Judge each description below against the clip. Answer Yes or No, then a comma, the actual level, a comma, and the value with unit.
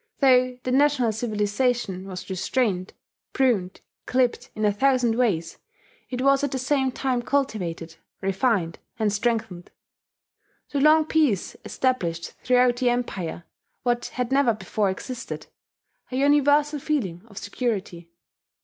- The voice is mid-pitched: No, high, 245 Hz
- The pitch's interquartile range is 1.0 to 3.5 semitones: No, average, 5.2 semitones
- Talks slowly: Yes, slow, 125 wpm